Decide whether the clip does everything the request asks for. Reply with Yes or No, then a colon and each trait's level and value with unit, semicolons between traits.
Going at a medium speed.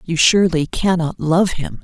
Yes: average, 165 wpm